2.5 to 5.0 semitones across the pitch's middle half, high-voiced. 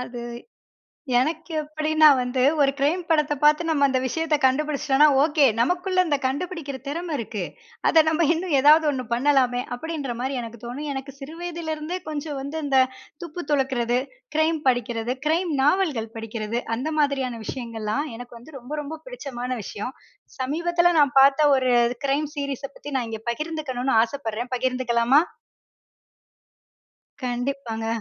Yes: average, 3.9 semitones; very high, 280 Hz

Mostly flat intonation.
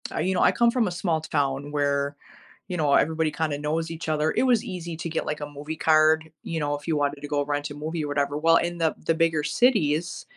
Yes: narrow, 2.2 semitones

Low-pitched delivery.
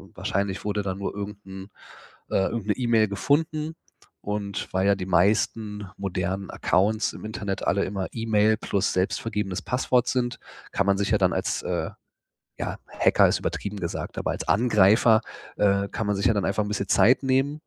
Yes: low, 105 Hz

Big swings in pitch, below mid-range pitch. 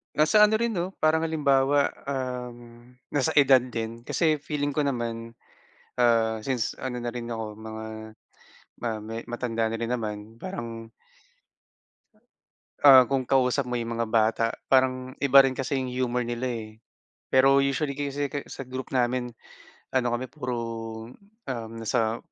No: average, 2.9 semitones; low, 125 Hz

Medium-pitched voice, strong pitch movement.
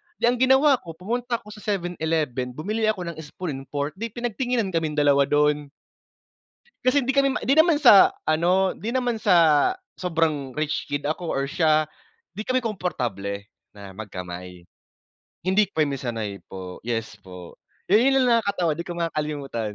Yes: medium, 160 Hz; wide, 7.7 semitones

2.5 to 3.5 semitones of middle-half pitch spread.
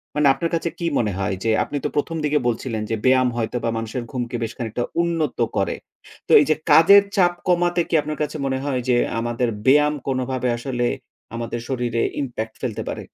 No: average, 4.3 semitones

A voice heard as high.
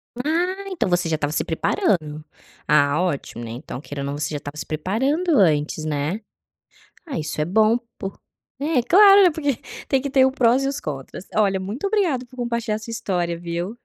Yes: high, 200 Hz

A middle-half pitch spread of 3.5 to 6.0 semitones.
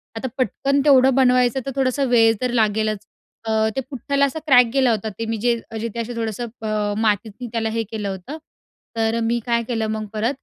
No: average, 2.7 semitones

